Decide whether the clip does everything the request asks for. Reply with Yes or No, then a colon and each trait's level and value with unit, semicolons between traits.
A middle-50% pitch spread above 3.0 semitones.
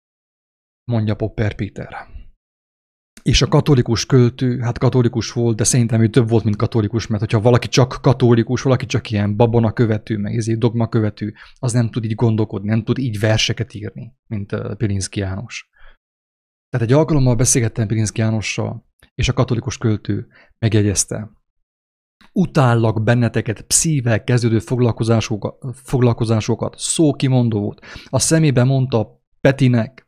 No: narrow, 2.4 semitones